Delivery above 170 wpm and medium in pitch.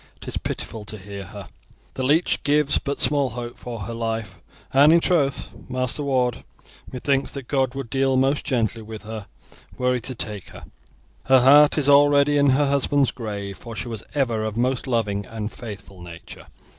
No: average, 190 wpm; low, 125 Hz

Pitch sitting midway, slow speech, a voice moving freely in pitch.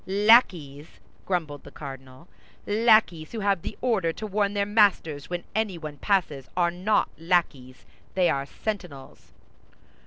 Yes: medium, 175 Hz; slow, 130 wpm; wide, 5.9 semitones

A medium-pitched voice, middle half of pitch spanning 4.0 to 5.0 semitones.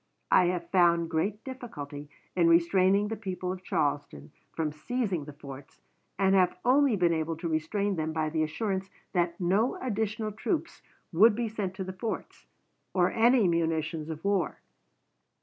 Yes: medium, 180 Hz; average, 4.5 semitones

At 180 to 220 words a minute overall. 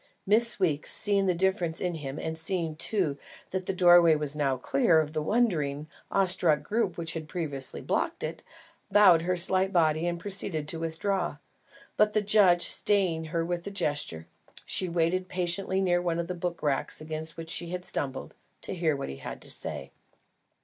Yes: average, 185 wpm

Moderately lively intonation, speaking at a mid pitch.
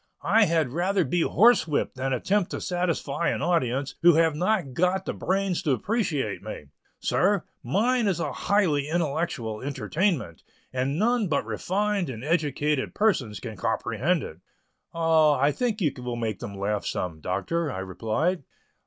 No: wide, 6.4 semitones; medium, 160 Hz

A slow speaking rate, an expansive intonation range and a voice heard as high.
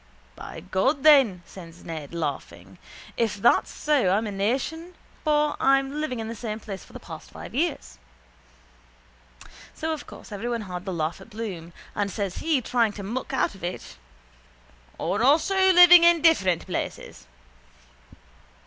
No: average, 155 wpm; wide, 8.0 semitones; high, 220 Hz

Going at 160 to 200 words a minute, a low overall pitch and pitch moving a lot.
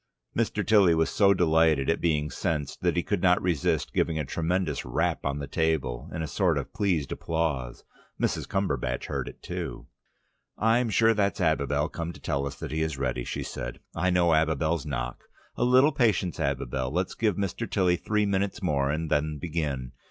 No: average, 190 wpm; very low, 80 Hz; average, 4.6 semitones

